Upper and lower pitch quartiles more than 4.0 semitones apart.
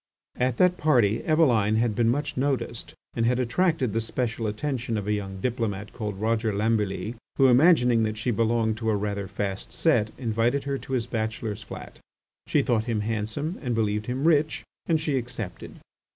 No: average, 3.3 semitones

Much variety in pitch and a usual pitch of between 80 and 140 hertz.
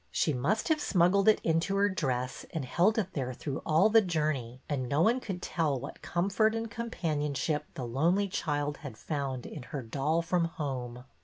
No: wide, 6.0 semitones; medium, 155 Hz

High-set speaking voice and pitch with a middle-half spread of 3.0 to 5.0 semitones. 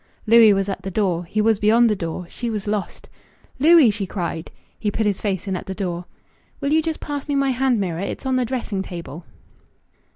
Yes: high, 210 Hz; average, 4.5 semitones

